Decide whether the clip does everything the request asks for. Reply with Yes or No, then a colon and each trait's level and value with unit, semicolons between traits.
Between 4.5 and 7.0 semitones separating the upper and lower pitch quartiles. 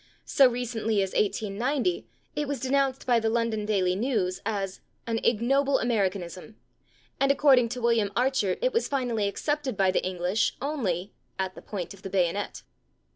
Yes: average, 5.1 semitones